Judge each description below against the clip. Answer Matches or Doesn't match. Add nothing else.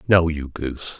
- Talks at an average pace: Matches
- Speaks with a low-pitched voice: Matches